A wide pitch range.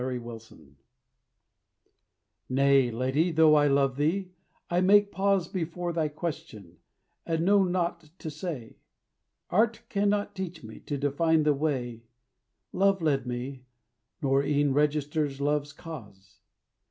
No: average, 4.5 semitones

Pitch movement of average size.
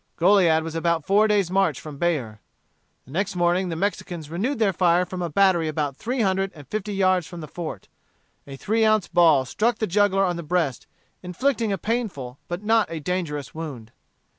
Yes: average, 4.1 semitones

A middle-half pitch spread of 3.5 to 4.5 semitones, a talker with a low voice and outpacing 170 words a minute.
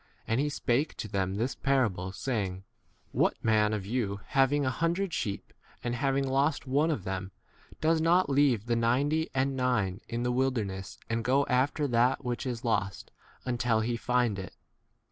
Yes: average, 4.2 semitones; low, 125 Hz; average, 185 wpm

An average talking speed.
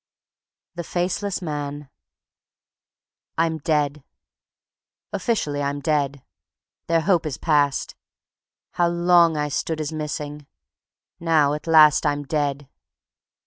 No: slow, 100 wpm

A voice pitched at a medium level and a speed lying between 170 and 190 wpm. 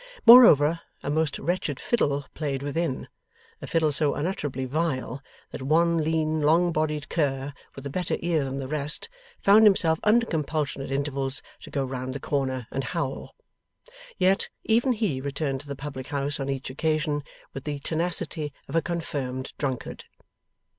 No: medium, 145 Hz; average, 160 wpm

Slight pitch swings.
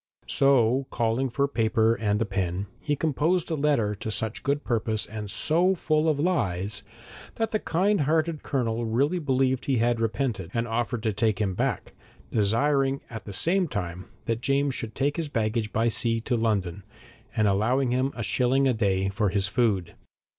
No: average, 4.5 semitones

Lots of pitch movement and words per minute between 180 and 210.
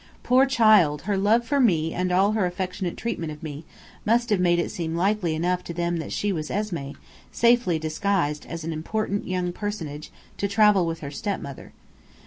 No: average, 4.3 semitones; average, 185 wpm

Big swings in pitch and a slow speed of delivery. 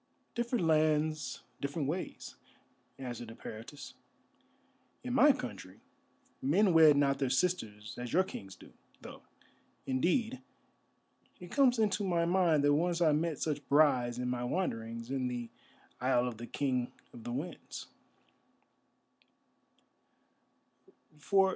Yes: wide, 6.1 semitones; slow, 120 wpm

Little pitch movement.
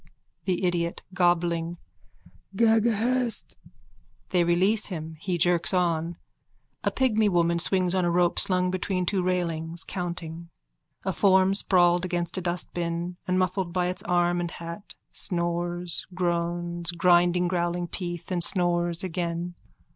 Yes: narrow, 1.2 semitones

